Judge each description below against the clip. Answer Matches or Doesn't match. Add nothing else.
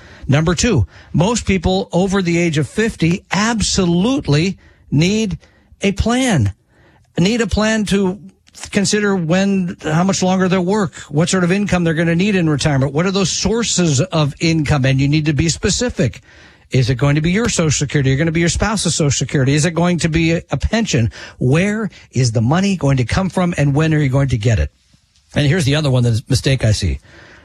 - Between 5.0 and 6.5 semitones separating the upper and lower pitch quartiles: Matches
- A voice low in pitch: Doesn't match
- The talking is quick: Matches